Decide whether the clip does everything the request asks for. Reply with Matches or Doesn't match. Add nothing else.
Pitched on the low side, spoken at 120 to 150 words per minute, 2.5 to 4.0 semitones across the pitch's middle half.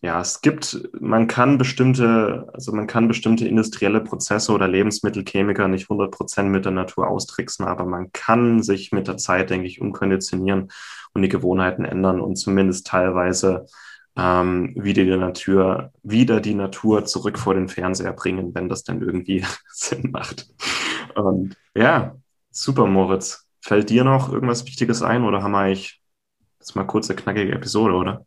Doesn't match